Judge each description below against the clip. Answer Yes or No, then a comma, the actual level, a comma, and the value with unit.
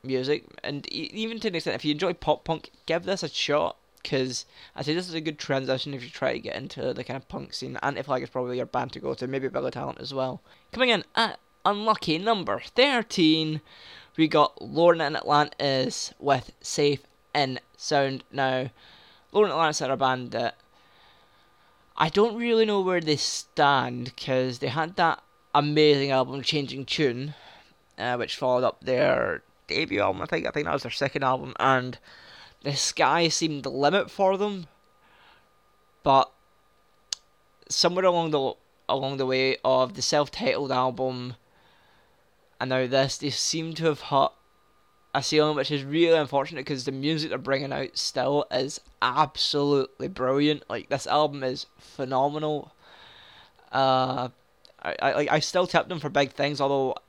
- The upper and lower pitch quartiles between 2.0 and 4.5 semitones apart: Yes, average, 3.6 semitones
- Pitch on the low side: No, medium, 145 Hz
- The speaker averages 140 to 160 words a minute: No, average, 170 wpm